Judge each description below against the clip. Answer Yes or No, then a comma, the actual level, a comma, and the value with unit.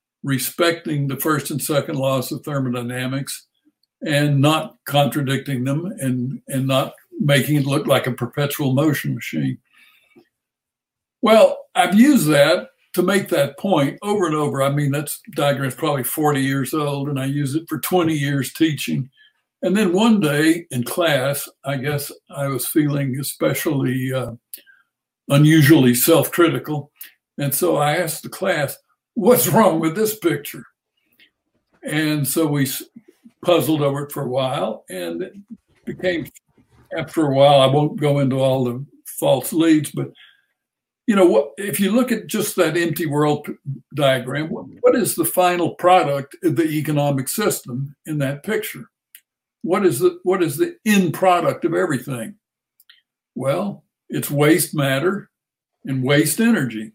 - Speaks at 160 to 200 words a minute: No, average, 150 wpm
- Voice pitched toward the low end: No, medium, 150 Hz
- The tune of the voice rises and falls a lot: No, average, 4.5 semitones